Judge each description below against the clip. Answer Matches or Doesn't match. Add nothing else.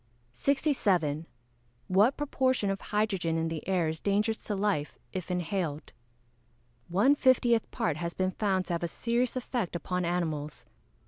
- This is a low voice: Doesn't match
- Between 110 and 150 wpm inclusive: Matches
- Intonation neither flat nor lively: Matches